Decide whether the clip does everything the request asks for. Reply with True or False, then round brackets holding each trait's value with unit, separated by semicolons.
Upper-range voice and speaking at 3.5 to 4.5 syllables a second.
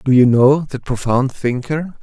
False (135 Hz; 4.1 syllables/s)